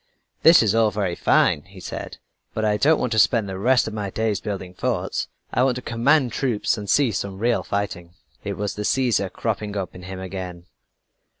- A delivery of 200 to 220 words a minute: Yes, fast, 205 wpm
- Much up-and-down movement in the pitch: No, average, 3.6 semitones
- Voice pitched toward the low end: Yes, low, 105 Hz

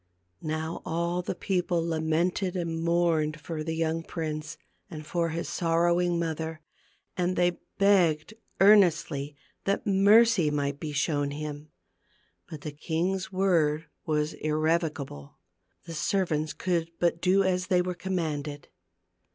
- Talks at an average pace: No, slow, 130 wpm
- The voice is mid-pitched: Yes, medium, 165 Hz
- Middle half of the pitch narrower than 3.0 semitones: Yes, narrow, 2.6 semitones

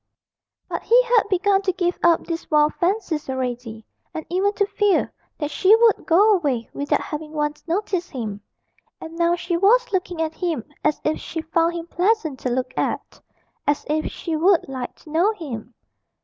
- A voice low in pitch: No, very high, 330 Hz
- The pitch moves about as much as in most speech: Yes, average, 4.3 semitones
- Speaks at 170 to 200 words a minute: Yes, average, 180 wpm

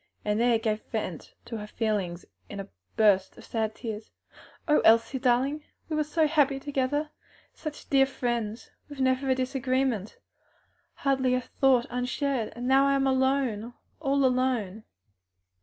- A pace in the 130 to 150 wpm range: Yes, average, 145 wpm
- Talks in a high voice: Yes, very high, 255 Hz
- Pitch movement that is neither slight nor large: Yes, average, 3.6 semitones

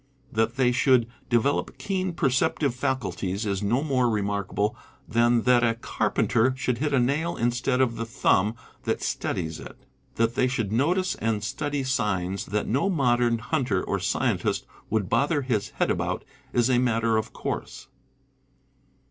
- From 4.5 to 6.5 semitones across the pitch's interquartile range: No, average, 3.3 semitones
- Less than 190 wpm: Yes, average, 155 wpm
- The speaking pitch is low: Yes, low, 120 Hz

